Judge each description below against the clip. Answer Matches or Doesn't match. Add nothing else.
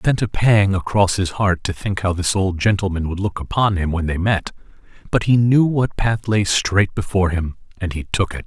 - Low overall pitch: Matches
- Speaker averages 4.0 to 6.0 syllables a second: Matches